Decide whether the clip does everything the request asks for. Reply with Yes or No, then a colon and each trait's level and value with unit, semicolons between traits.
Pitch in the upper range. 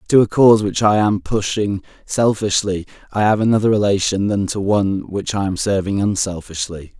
No: low, 100 Hz